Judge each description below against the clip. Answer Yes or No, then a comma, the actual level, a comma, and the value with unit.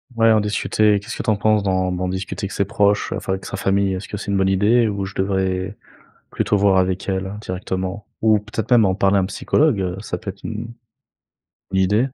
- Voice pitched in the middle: No, low, 100 Hz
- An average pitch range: No, narrow, 1.9 semitones